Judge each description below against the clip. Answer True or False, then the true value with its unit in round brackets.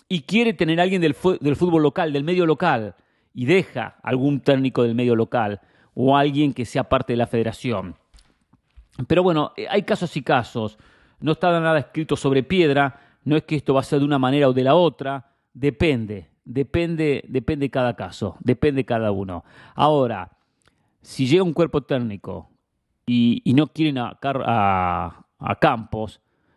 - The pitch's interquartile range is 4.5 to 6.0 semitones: True (4.9 semitones)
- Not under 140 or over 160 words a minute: False (170 wpm)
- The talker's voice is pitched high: False (135 Hz)